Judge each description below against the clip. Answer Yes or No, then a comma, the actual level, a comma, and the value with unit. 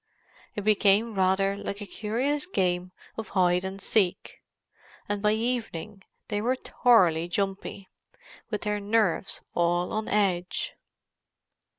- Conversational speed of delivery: No, slow, 120 wpm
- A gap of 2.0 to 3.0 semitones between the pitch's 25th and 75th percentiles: Yes, average, 2.7 semitones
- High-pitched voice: Yes, high, 200 Hz